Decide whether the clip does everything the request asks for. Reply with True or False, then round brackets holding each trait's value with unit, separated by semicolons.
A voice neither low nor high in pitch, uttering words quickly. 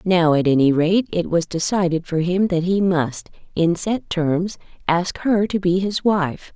False (175 Hz; 190 wpm)